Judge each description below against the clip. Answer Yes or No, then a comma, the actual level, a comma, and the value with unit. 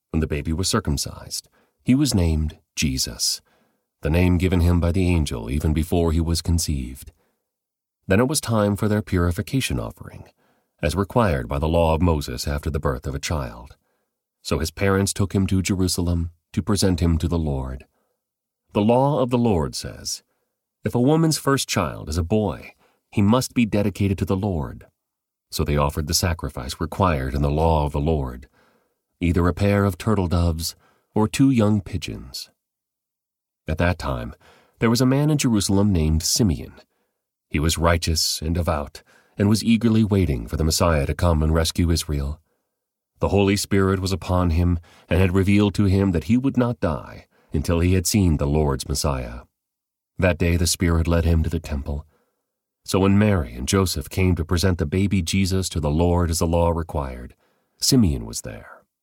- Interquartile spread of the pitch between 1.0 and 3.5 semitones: No, average, 4.1 semitones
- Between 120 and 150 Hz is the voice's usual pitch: No, very low, 85 Hz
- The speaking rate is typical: Yes, average, 180 wpm